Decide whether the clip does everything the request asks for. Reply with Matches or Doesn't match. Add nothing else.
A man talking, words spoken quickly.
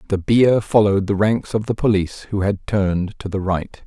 Matches